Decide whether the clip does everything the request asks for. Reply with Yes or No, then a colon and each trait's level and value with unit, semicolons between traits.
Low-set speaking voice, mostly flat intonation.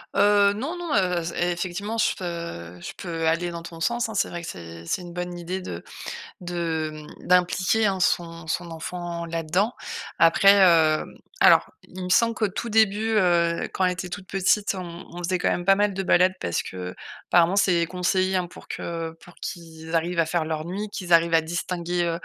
No: medium, 175 Hz; narrow, 2.2 semitones